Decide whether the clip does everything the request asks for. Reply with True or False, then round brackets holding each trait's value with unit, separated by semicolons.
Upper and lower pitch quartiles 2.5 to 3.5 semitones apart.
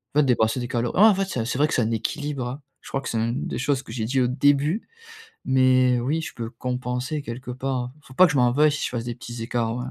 True (2.8 semitones)